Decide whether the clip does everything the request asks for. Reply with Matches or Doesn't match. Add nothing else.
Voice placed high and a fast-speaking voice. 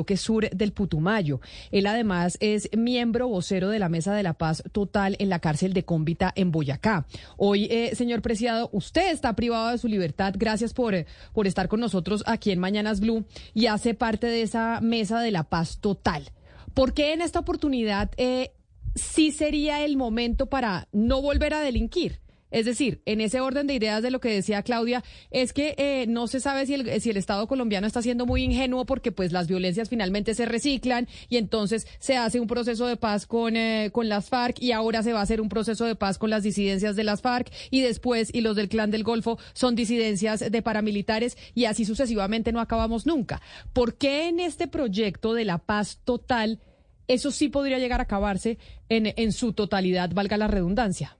Matches